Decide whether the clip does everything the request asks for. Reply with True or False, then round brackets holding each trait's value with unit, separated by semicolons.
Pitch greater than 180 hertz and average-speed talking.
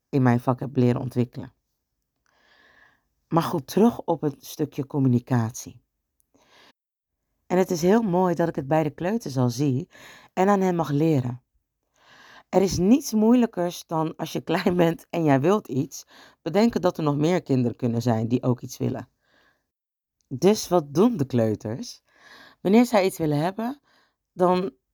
False (160 Hz; 160 wpm)